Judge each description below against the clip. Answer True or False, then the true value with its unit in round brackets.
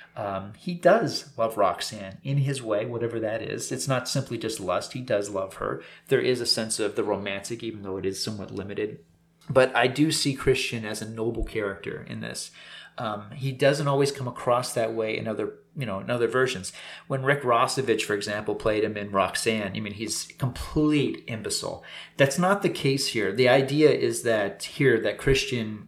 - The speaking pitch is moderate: False (115 Hz)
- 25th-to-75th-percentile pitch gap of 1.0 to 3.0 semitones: False (4.4 semitones)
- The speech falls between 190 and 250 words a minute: True (195 wpm)